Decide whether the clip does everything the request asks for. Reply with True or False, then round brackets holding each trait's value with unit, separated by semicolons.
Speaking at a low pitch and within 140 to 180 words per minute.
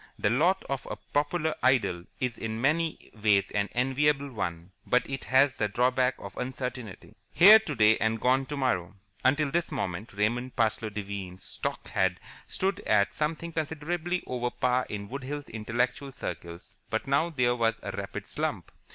True (125 Hz; 160 wpm)